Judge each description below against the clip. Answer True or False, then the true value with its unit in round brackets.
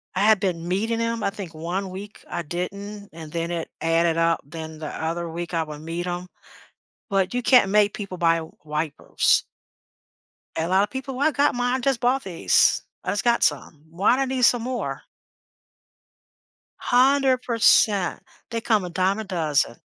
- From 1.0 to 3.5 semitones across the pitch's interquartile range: False (5.6 semitones)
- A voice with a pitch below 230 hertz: True (190 Hz)